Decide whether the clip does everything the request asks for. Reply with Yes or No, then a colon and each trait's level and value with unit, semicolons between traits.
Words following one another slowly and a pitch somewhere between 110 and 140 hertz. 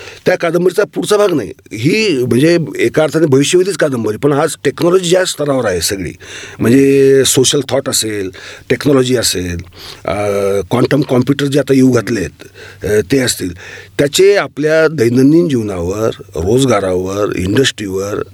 No: fast, 130 wpm; low, 135 Hz